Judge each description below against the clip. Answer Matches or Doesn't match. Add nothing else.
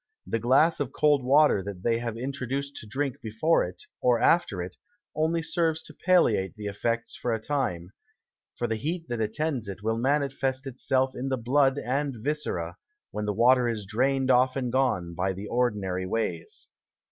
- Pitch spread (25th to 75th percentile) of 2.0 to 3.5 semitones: Doesn't match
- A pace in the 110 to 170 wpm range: Doesn't match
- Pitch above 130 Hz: Doesn't match